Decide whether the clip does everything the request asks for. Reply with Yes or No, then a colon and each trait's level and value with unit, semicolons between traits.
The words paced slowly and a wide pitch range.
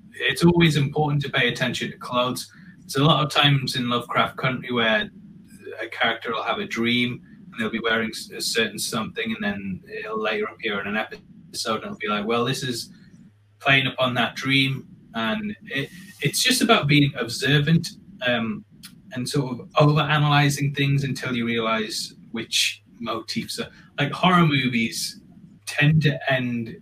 No: average, 170 wpm; wide, 6.8 semitones